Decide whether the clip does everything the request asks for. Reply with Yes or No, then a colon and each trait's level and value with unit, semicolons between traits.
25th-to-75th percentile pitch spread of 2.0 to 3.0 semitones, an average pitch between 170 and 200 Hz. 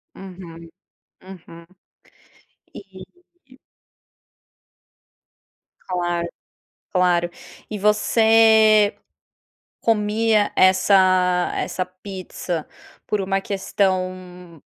Yes: narrow, 2.6 semitones; high, 190 Hz